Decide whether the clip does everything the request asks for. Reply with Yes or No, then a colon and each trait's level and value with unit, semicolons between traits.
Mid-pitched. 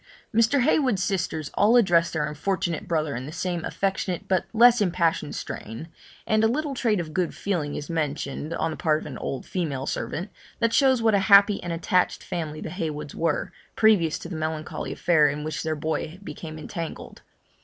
Yes: medium, 170 Hz